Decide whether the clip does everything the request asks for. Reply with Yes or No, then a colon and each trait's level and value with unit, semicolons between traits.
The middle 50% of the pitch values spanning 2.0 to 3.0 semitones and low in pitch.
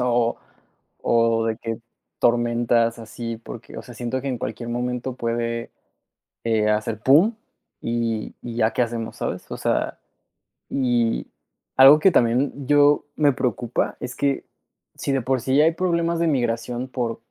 Yes: narrow, 2.5 semitones; low, 120 Hz